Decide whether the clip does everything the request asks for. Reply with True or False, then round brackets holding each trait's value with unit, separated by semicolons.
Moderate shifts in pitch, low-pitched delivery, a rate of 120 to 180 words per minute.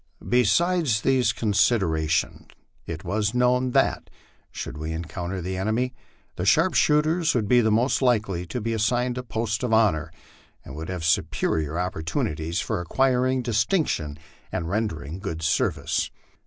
False (6.8 semitones; 105 Hz; 140 wpm)